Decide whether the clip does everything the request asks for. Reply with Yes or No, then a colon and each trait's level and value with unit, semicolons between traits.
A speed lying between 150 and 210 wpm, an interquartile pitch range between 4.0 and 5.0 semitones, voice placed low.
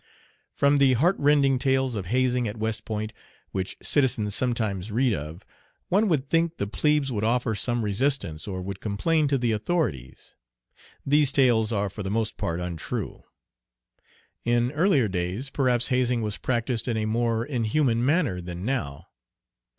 Yes: average, 155 wpm; average, 4.6 semitones; low, 120 Hz